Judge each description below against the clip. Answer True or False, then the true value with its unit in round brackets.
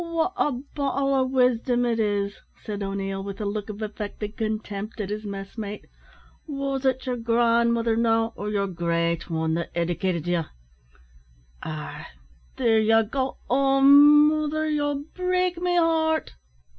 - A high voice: True (230 Hz)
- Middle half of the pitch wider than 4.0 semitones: True (5.5 semitones)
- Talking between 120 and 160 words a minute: True (145 wpm)